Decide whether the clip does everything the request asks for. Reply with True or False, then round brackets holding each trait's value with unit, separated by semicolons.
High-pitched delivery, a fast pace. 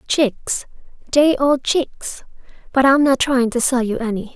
False (260 Hz; 165 wpm)